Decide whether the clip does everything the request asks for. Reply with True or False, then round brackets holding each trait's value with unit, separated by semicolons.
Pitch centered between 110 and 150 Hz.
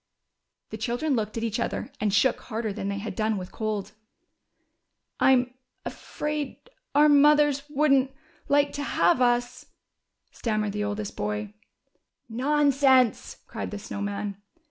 False (235 Hz)